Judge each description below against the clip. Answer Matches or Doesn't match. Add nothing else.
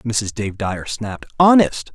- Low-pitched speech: Matches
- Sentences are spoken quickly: Doesn't match